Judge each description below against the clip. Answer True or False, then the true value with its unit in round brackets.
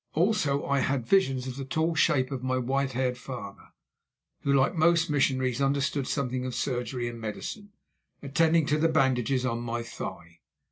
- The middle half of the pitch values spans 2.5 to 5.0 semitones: True (2.9 semitones)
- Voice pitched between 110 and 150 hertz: True (135 Hz)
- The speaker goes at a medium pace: True (170 wpm)